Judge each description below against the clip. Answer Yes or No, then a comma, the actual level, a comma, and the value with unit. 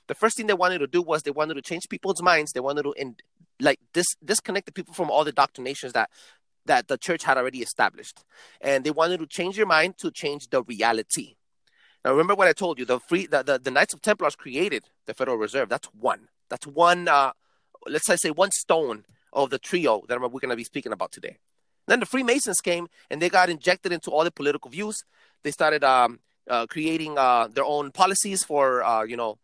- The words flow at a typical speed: No, fast, 220 wpm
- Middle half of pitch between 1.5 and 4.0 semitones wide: No, average, 4.9 semitones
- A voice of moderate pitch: Yes, medium, 160 Hz